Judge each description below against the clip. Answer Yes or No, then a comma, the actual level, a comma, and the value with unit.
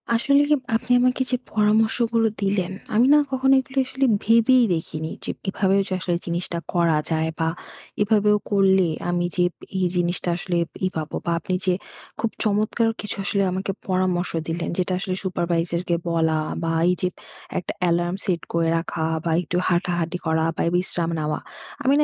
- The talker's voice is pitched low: No, medium, 185 Hz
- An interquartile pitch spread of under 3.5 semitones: No, average, 3.8 semitones